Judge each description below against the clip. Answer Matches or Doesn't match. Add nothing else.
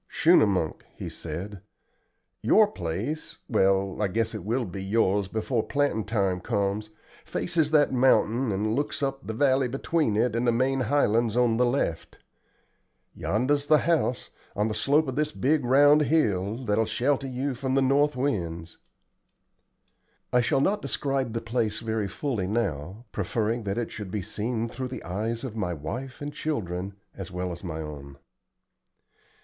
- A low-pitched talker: Matches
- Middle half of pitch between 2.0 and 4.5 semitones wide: Doesn't match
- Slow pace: Doesn't match